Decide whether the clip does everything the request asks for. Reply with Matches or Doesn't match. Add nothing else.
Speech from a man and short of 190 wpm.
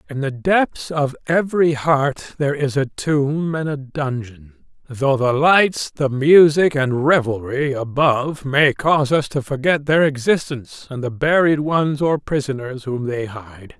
Matches